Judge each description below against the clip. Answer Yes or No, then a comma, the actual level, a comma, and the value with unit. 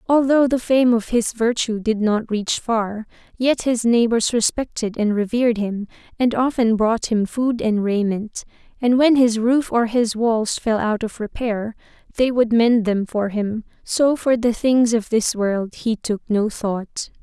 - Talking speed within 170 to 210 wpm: Yes, average, 180 wpm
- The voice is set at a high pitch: Yes, high, 230 Hz